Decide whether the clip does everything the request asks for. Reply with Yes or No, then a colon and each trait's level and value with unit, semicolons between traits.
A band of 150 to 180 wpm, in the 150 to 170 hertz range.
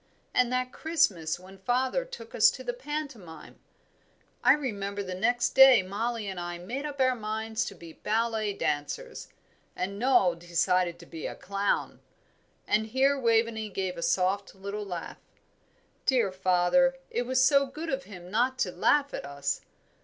No: average, 160 wpm; high, 215 Hz